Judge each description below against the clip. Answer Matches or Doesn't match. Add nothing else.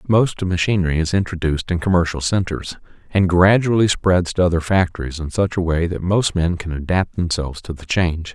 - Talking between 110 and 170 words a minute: Doesn't match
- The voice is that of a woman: Doesn't match